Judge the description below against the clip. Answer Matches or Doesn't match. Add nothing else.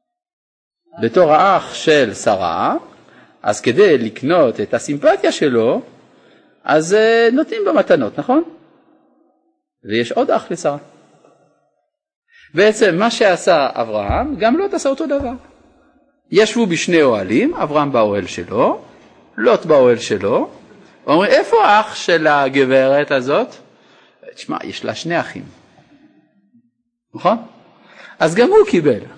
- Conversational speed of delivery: Matches